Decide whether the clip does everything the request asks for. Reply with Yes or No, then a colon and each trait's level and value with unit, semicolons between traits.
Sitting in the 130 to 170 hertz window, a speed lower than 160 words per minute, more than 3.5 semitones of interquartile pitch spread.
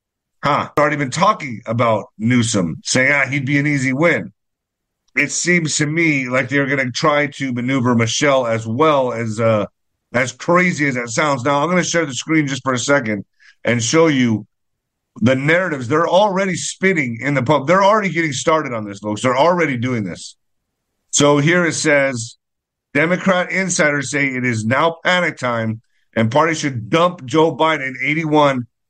No: medium, 140 Hz; average, 180 wpm; average, 4.7 semitones